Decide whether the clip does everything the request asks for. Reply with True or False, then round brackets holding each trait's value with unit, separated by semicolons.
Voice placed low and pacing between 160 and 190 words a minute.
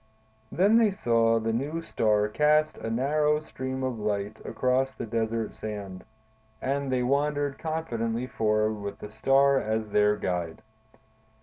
False (115 Hz; 140 wpm)